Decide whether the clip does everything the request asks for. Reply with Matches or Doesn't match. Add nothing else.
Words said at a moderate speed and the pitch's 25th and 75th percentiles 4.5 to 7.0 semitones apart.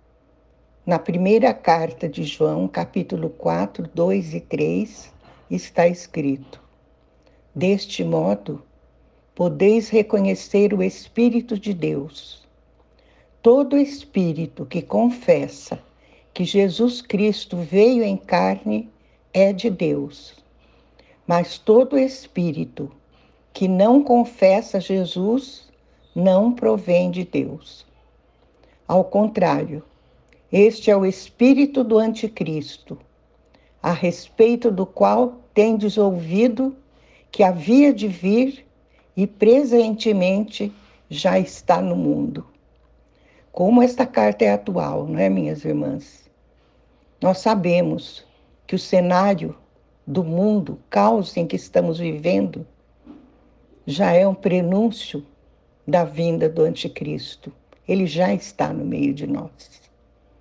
Doesn't match